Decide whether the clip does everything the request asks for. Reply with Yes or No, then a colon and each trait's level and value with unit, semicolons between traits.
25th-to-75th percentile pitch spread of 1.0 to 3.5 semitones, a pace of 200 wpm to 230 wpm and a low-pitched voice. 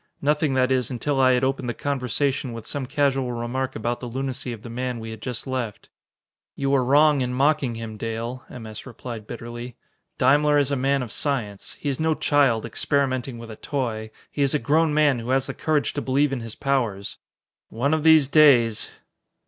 Yes: average, 3.1 semitones; fast, 205 wpm; low, 130 Hz